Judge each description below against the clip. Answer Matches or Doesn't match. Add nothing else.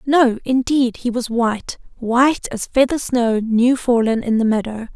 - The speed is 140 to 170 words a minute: Matches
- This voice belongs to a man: Doesn't match